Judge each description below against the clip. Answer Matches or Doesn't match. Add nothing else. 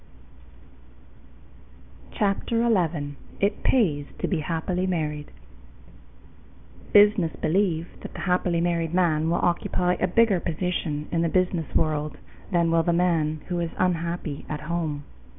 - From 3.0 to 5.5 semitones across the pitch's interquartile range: Doesn't match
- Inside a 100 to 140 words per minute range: Matches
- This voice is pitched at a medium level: Matches